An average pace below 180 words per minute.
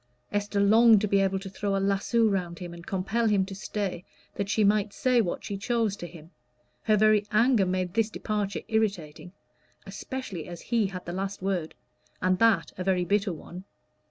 No: average, 190 wpm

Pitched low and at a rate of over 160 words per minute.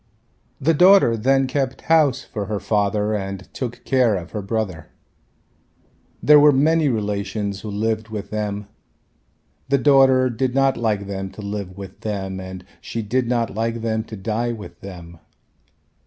No: low, 110 Hz; average, 155 wpm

